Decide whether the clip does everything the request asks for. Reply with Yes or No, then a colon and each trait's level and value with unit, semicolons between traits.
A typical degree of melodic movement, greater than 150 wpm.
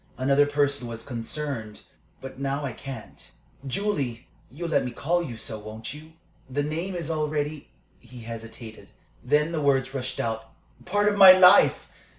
Yes: average, 4.7 semitones; average, 160 wpm